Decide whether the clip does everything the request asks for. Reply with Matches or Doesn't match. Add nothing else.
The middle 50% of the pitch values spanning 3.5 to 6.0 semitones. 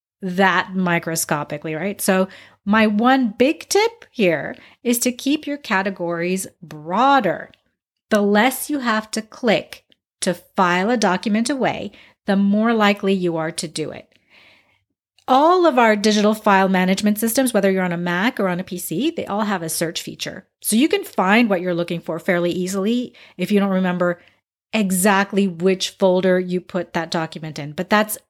Matches